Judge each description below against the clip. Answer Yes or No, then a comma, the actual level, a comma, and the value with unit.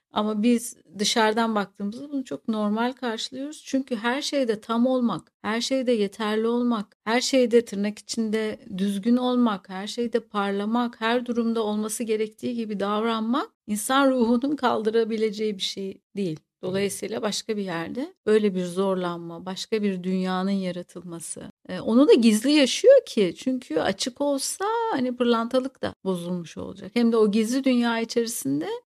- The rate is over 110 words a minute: Yes, fast, 140 wpm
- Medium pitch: No, high, 225 Hz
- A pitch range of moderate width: Yes, average, 3.5 semitones